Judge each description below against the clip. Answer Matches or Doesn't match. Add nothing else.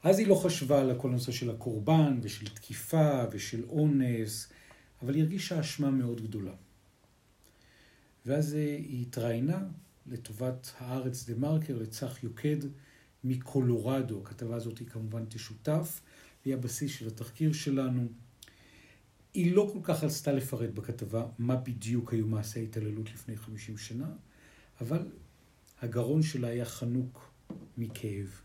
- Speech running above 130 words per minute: Doesn't match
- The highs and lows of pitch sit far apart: Doesn't match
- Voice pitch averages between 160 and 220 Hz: Doesn't match